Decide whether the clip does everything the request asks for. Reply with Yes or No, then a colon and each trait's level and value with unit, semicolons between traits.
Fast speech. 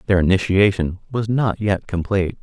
No: average, 150 wpm